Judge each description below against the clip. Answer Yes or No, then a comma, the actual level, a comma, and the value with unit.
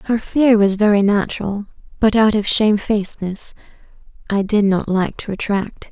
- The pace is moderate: Yes, average, 150 wpm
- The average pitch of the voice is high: Yes, high, 205 Hz